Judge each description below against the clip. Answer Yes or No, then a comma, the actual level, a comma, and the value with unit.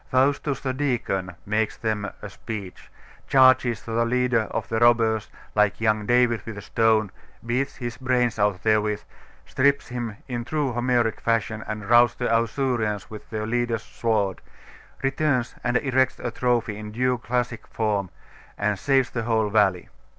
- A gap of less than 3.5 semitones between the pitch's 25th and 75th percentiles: Yes, average, 2.7 semitones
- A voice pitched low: Yes, low, 115 Hz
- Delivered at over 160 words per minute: No, average, 155 wpm